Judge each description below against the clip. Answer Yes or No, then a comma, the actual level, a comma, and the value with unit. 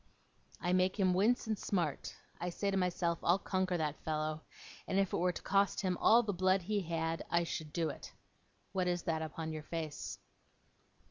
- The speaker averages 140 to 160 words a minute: No, average, 195 wpm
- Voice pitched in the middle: Yes, medium, 180 Hz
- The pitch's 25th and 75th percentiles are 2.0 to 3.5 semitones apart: Yes, average, 2.8 semitones